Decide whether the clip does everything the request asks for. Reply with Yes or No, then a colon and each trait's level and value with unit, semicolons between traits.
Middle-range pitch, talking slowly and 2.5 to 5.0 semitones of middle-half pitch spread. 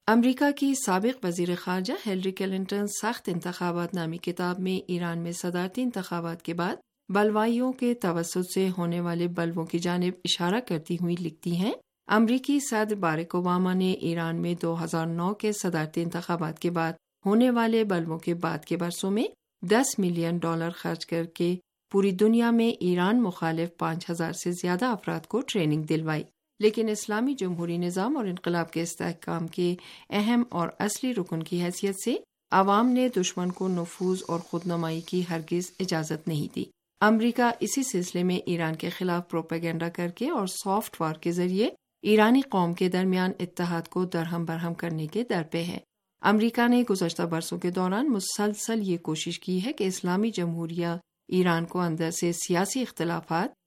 No: medium, 180 Hz; average, 170 wpm; average, 3.4 semitones